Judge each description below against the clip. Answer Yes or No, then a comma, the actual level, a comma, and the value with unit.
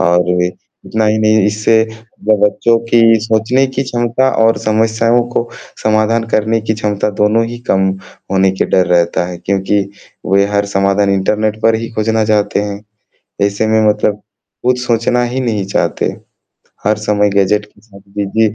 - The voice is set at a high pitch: No, low, 110 Hz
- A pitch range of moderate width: No, narrow, 2.0 semitones